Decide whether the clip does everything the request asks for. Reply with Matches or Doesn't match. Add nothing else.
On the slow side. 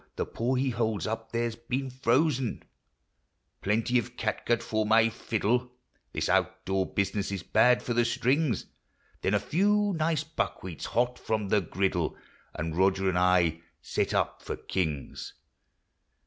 Doesn't match